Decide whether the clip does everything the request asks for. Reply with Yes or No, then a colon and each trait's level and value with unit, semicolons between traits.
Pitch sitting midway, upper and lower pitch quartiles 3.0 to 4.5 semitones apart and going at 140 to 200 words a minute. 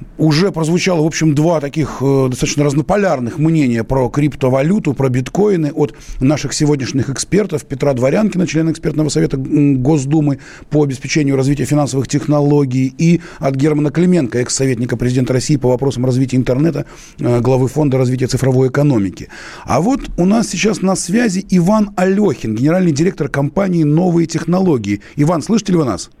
Yes: medium, 150 Hz; average, 4.2 semitones; average, 145 wpm